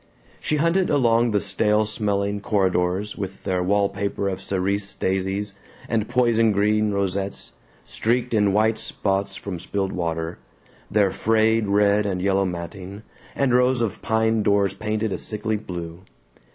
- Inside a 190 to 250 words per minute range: No, average, 140 wpm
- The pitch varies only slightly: Yes, narrow, 2.2 semitones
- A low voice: Yes, low, 100 Hz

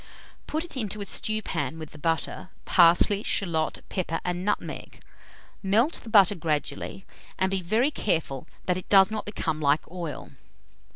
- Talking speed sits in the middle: Yes, average, 155 wpm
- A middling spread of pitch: Yes, average, 4.3 semitones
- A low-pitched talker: No, medium, 185 Hz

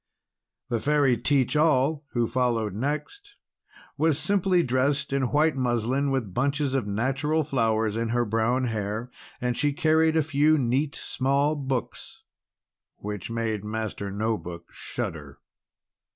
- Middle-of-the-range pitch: No, low, 130 Hz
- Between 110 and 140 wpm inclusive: Yes, slow, 135 wpm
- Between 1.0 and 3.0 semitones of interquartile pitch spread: No, average, 4.5 semitones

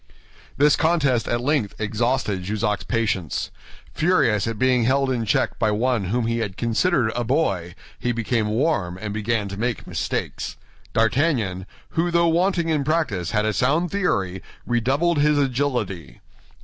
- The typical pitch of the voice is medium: No, low, 120 Hz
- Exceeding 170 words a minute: No, average, 150 wpm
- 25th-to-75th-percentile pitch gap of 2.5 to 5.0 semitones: No, wide, 5.4 semitones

